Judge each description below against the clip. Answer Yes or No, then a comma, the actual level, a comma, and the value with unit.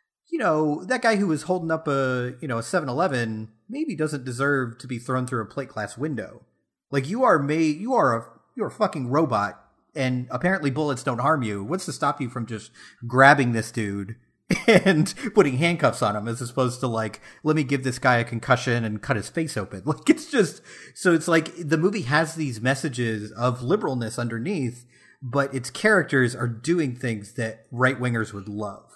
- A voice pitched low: Yes, low, 130 Hz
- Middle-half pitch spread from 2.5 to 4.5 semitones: No, average, 5.0 semitones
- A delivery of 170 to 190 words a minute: No, average, 200 wpm